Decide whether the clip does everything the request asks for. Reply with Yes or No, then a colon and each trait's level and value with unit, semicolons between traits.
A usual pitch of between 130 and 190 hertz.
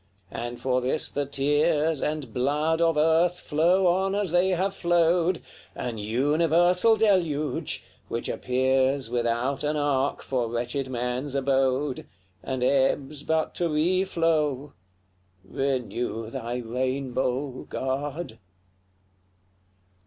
Yes: medium, 140 Hz